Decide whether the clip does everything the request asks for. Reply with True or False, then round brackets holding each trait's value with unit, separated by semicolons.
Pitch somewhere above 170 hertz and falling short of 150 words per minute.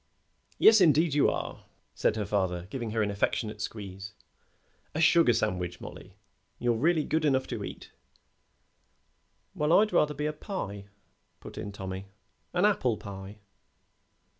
False (115 Hz; 140 wpm)